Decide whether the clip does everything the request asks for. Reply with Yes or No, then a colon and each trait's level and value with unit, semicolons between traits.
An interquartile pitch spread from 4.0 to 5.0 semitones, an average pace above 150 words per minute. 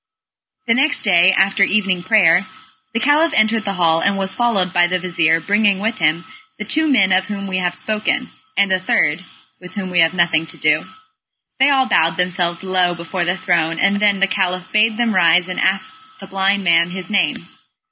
No: average, 2.9 semitones; average, 200 wpm